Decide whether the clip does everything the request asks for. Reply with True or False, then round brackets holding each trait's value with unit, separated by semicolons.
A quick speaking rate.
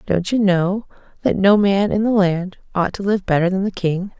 True (230 wpm)